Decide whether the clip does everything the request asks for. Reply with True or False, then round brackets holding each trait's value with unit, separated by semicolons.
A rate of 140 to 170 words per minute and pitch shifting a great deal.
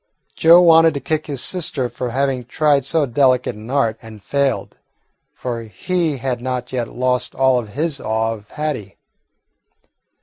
False (160 wpm; 3.8 semitones)